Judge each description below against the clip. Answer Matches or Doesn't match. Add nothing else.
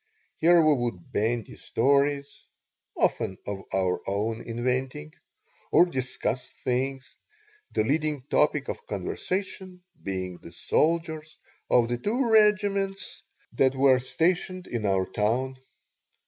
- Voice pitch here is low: Matches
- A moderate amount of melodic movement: Doesn't match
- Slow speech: Matches